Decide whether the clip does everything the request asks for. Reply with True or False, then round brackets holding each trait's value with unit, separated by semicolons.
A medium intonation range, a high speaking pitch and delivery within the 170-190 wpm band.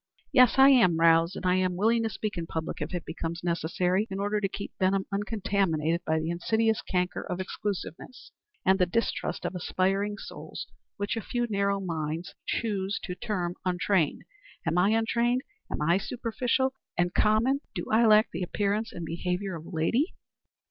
True (3.8 semitones; 195 Hz; 175 wpm)